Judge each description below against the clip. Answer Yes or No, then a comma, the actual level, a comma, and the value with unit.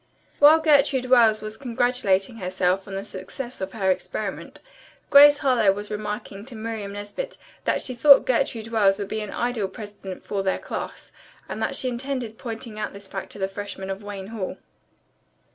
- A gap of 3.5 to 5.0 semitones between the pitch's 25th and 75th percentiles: Yes, average, 4.0 semitones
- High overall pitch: Yes, high, 215 Hz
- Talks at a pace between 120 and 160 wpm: No, average, 175 wpm